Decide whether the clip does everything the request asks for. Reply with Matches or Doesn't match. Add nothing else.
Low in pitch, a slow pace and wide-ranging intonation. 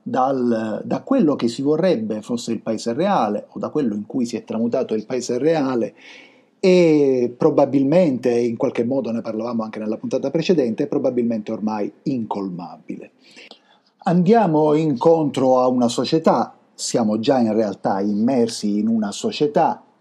Doesn't match